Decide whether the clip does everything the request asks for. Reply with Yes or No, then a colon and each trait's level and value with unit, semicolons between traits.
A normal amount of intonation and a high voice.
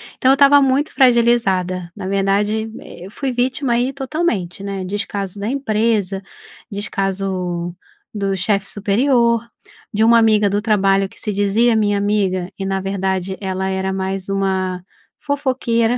Yes: average, 3.5 semitones; high, 205 Hz